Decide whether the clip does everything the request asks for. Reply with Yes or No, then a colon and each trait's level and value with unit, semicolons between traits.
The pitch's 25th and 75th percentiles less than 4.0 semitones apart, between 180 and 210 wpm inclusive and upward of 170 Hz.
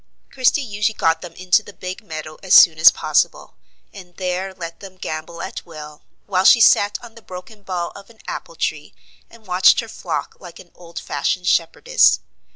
Yes: average, 3.4 semitones; average, 185 wpm; medium, 185 Hz